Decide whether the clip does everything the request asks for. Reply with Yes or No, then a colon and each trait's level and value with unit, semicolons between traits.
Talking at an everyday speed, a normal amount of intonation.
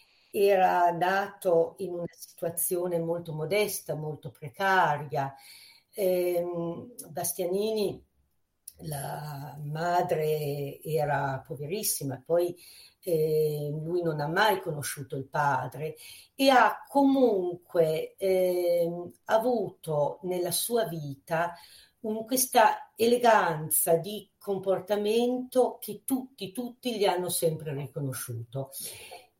No: slow, 90 wpm; average, 4.7 semitones